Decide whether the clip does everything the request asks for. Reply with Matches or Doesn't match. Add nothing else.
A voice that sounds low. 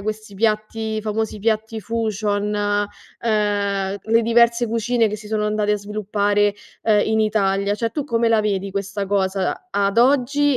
Doesn't match